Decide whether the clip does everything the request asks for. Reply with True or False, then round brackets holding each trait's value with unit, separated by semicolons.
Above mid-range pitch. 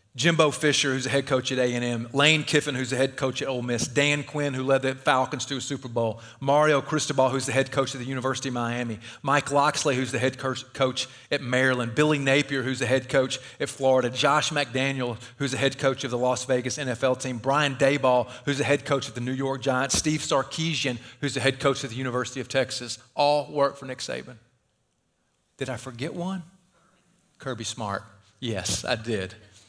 False (135 Hz)